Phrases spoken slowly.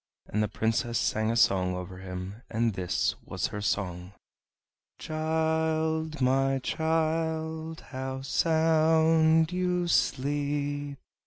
Yes: slow, 105 wpm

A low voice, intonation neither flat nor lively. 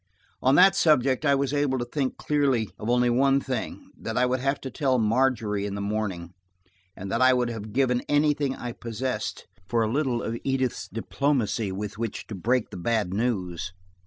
Yes: low, 125 Hz; average, 3.8 semitones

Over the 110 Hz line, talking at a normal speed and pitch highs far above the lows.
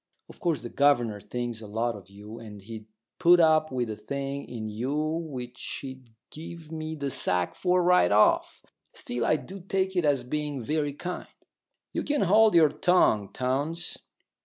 Yes: medium, 140 Hz; average, 180 wpm; wide, 6.0 semitones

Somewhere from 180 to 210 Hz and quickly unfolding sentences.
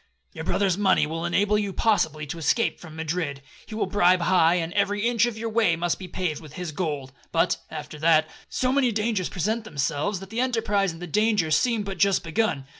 Yes: medium, 185 Hz; fast, 210 wpm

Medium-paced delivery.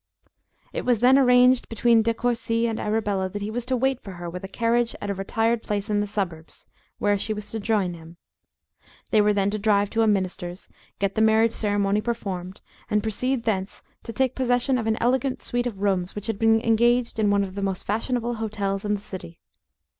No: fast, 210 wpm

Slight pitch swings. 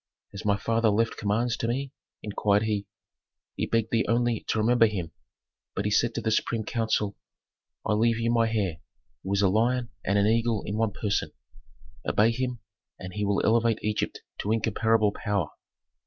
Yes: narrow, 2.1 semitones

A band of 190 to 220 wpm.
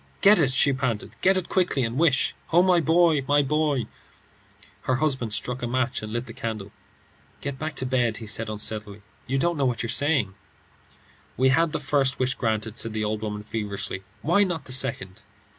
Yes: average, 200 wpm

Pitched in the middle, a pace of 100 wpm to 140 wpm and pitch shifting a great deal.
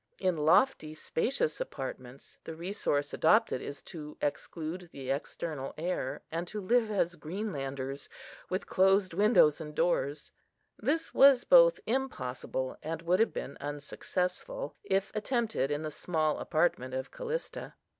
Yes: medium, 170 Hz; slow, 135 wpm; wide, 6.4 semitones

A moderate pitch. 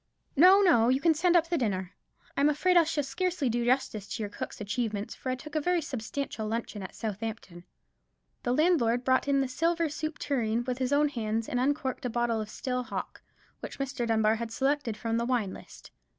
No: very high, 250 Hz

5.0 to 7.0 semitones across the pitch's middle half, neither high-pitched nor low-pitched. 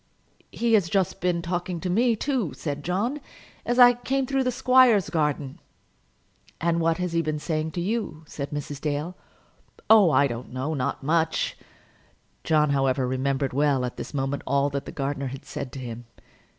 Yes: wide, 5.4 semitones; medium, 155 Hz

